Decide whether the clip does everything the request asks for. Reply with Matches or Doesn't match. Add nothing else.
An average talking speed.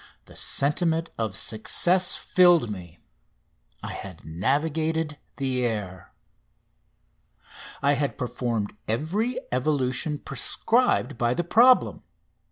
Doesn't match